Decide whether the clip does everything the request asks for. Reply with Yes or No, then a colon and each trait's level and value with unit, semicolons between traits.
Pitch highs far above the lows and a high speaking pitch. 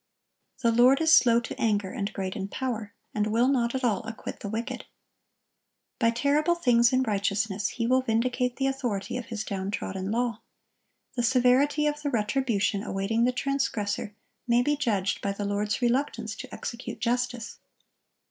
No: average, 3.7 semitones; high, 235 Hz